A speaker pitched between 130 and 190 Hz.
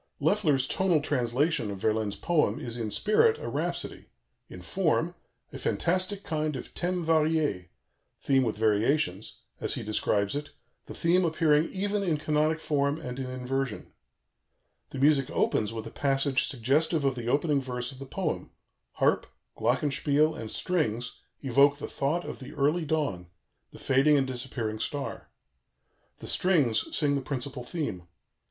Yes: medium, 140 Hz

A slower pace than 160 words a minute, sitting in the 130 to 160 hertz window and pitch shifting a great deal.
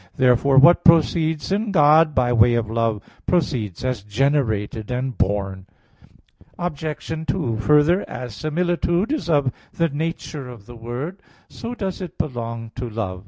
Yes: average, 145 wpm; low, 135 Hz; wide, 6.2 semitones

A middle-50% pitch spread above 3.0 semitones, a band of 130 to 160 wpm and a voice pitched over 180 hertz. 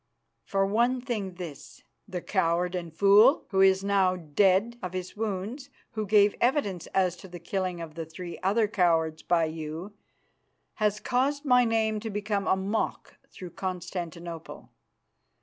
Yes: average, 3.6 semitones; average, 150 wpm; high, 190 Hz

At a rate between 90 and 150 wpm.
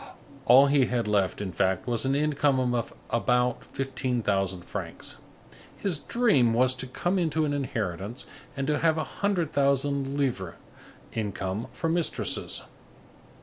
Yes: average, 145 wpm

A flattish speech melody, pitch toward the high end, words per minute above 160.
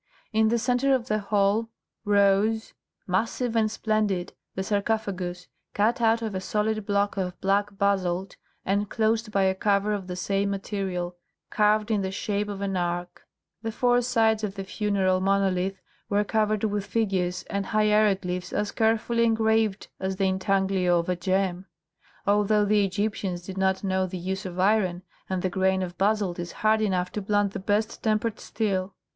Yes: narrow, 2.3 semitones; high, 200 Hz; average, 170 wpm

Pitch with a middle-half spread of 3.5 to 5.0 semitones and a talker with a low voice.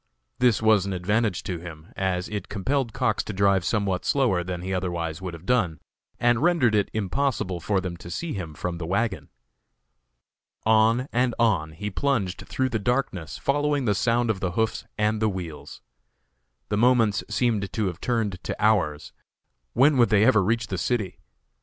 Yes: average, 4.5 semitones; low, 105 Hz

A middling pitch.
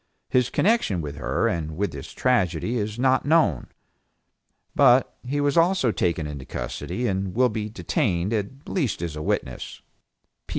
No: low, 110 Hz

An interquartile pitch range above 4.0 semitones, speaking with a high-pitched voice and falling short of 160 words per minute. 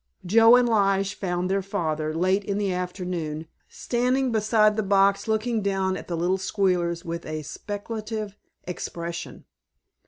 No: average, 3.4 semitones; high, 195 Hz; average, 145 wpm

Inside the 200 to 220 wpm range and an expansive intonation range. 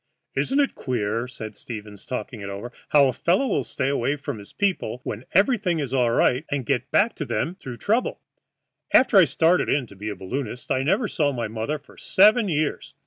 Yes: fast, 205 wpm; wide, 7.2 semitones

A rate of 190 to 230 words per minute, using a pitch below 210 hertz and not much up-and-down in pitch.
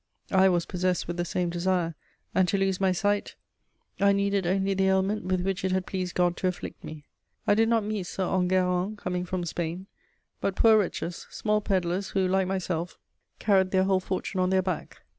Yes: average, 200 wpm; medium, 185 Hz; narrow, 1.4 semitones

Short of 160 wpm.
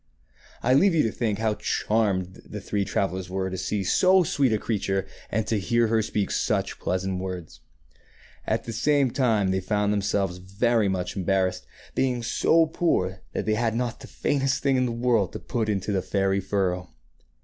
No: average, 185 wpm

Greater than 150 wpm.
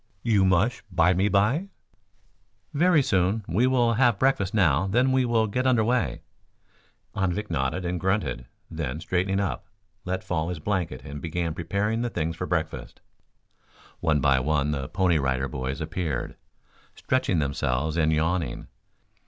No: average, 145 wpm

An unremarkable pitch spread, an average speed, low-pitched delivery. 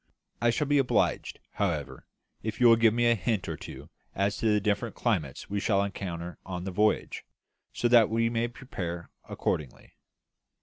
Yes: average, 4.7 semitones; average, 175 wpm; low, 105 Hz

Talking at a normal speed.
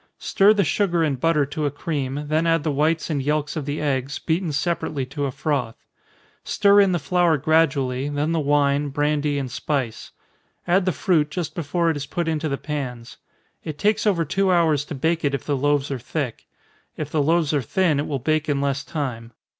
No: fast, 210 wpm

